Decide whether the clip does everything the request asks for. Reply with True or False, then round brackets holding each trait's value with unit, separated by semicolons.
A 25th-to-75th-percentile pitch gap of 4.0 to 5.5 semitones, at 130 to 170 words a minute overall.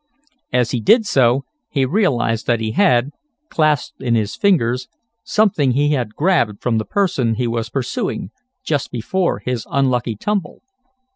True (4.8 semitones; 150 wpm)